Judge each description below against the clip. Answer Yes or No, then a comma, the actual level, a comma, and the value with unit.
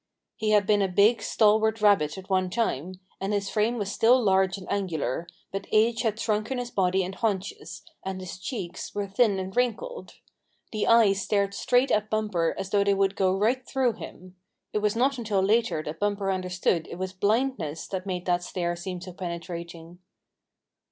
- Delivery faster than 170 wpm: Yes, average, 185 wpm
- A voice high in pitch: Yes, high, 195 Hz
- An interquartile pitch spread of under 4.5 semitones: Yes, average, 2.9 semitones